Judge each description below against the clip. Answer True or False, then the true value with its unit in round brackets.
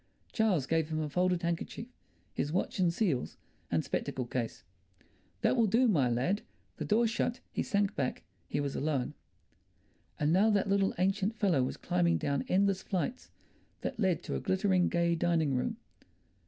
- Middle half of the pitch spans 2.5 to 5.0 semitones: False (5.6 semitones)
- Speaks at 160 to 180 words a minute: True (170 wpm)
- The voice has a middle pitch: True (175 Hz)